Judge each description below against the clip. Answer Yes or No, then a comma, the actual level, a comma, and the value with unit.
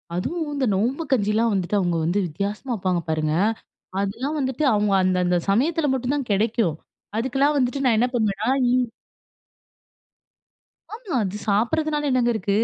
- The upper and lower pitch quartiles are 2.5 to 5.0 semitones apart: No, wide, 5.5 semitones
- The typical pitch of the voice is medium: No, high, 225 Hz